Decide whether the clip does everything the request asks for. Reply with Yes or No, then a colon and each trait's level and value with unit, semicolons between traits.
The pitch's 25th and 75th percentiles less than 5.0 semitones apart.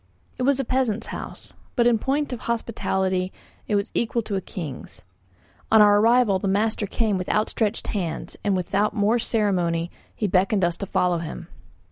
Yes: average, 3.7 semitones